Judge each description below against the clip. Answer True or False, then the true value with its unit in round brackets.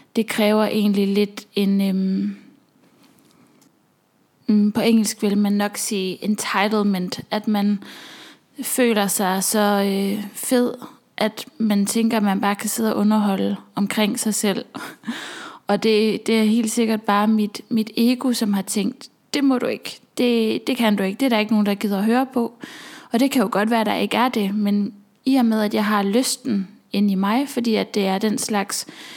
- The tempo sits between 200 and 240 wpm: False (190 wpm)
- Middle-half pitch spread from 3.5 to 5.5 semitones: False (2.9 semitones)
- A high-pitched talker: True (215 Hz)